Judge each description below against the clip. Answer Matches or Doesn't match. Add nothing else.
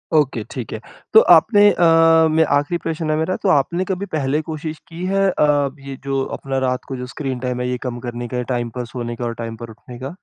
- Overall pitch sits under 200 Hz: Matches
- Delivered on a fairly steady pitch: Doesn't match